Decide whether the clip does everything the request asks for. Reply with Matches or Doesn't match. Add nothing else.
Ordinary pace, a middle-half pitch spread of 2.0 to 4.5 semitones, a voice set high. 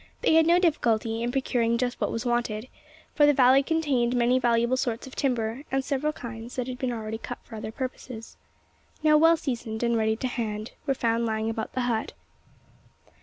Matches